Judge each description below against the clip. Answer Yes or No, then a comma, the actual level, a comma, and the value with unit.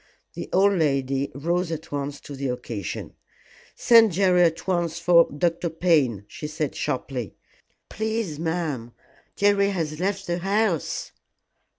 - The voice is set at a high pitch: No, medium, 165 Hz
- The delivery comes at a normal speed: No, slow, 130 wpm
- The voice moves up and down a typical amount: Yes, average, 4.6 semitones